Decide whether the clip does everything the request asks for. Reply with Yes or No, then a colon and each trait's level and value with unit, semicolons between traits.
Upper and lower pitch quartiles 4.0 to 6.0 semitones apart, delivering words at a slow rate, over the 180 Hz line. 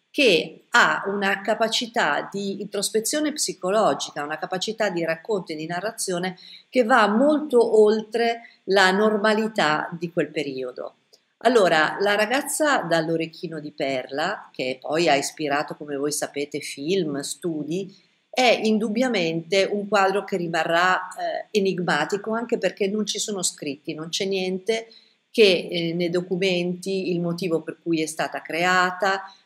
No: average, 4.5 semitones; average, 135 wpm; high, 190 Hz